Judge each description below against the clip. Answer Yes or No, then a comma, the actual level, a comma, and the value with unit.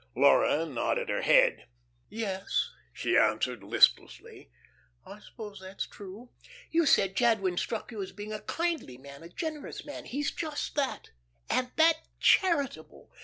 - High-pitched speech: Yes, high, 220 Hz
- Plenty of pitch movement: Yes, wide, 7.5 semitones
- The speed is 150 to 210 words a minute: No, average, 140 wpm